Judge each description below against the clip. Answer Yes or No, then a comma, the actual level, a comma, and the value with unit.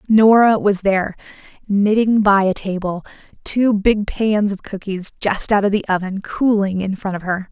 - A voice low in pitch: No, high, 200 Hz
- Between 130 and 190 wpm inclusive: Yes, average, 175 wpm